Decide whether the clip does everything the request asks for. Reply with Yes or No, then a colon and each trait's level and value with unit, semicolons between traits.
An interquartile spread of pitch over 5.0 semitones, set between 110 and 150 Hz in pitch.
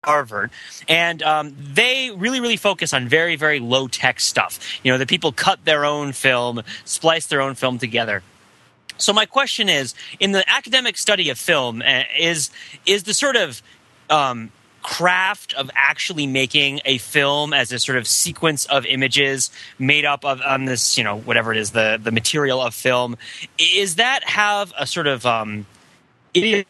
Yes: wide, 5.4 semitones; medium, 140 Hz